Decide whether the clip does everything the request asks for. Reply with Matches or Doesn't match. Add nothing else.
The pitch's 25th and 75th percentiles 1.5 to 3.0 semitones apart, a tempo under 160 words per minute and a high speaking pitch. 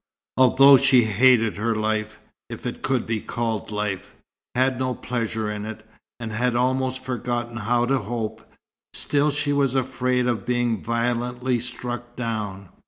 Doesn't match